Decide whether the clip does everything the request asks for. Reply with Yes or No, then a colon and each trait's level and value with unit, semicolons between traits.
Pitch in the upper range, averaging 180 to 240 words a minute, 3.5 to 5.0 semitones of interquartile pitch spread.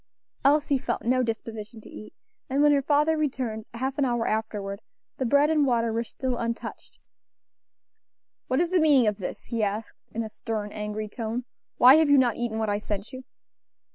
Yes: high, 235 Hz; average, 190 wpm; average, 4.0 semitones